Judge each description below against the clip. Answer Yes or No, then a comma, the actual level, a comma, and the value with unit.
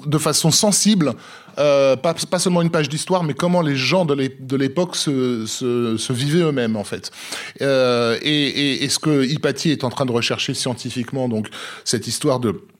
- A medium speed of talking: Yes, average, 190 wpm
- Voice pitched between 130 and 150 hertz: Yes, medium, 140 Hz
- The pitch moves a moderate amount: Yes, average, 4.1 semitones